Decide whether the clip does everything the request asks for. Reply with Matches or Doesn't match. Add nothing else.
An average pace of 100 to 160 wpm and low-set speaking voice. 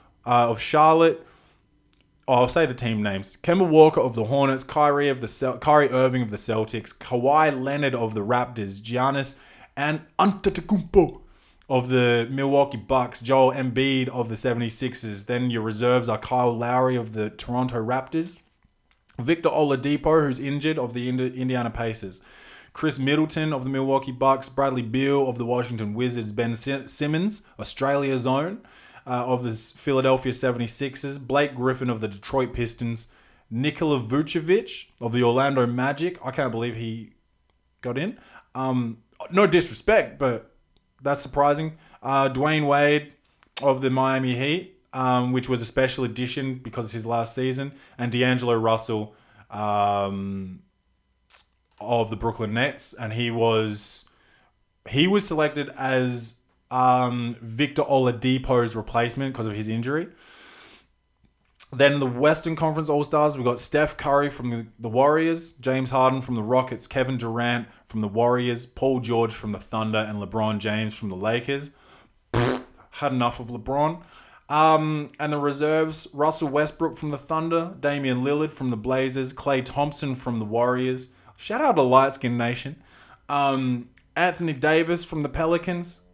Matches